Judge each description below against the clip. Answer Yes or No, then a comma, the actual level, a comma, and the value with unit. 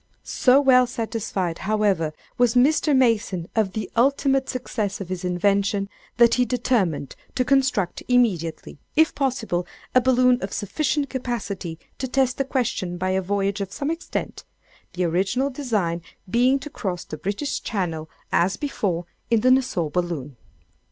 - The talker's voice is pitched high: Yes, high, 215 Hz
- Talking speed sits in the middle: Yes, average, 145 wpm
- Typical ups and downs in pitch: No, wide, 5.7 semitones